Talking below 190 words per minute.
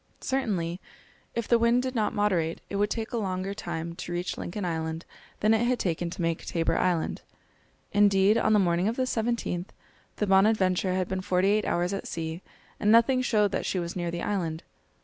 No: average, 200 wpm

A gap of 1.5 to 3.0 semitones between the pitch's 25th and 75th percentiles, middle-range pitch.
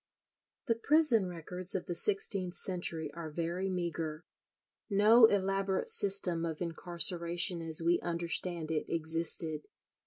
Yes: average, 2.7 semitones; medium, 175 Hz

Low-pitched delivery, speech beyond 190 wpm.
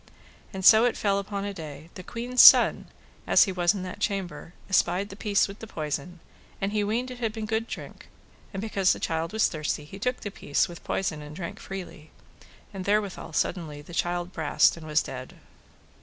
No: high, 190 Hz; average, 200 wpm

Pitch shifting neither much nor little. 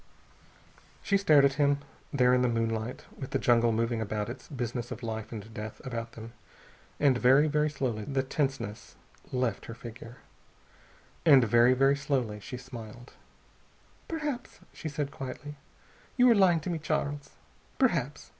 Yes: average, 3.9 semitones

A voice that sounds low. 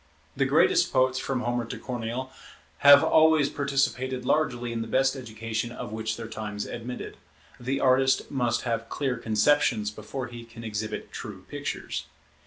Yes: low, 120 Hz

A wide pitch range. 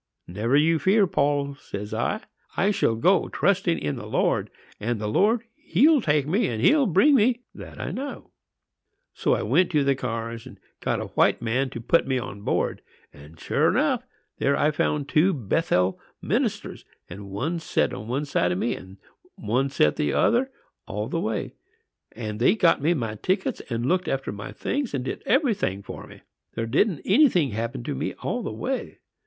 Yes: wide, 9.0 semitones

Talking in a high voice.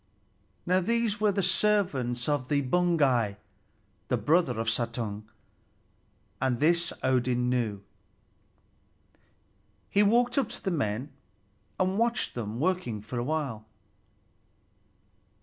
No: medium, 140 Hz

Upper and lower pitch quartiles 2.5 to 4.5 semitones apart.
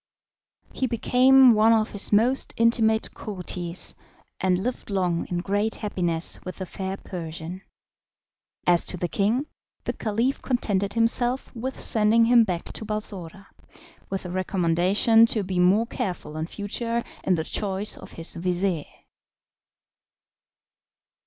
Yes: average, 4.2 semitones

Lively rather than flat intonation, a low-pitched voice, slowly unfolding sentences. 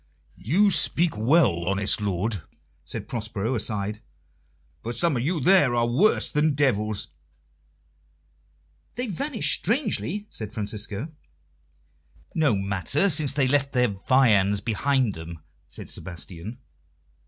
Yes: wide, 6.6 semitones; low, 120 Hz; slow, 115 wpm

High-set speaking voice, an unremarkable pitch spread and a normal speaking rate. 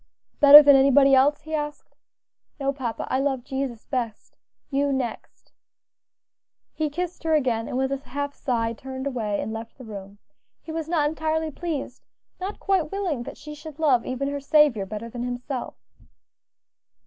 Yes: very high, 275 Hz; average, 3.5 semitones; average, 165 wpm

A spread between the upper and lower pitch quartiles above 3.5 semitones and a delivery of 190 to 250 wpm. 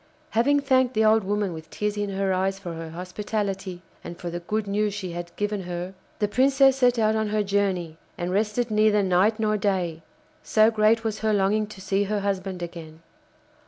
No: average, 2.8 semitones; average, 195 wpm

